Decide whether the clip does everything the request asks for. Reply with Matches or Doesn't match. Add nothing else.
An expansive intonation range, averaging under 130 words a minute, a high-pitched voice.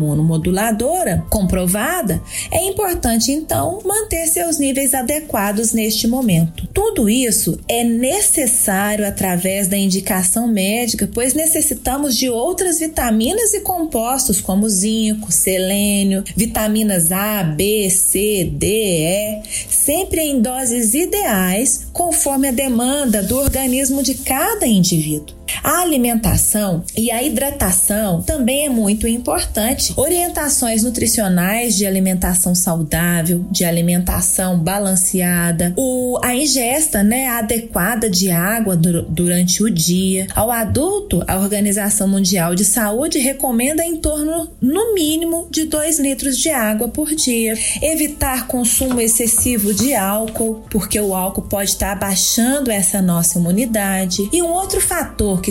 Matches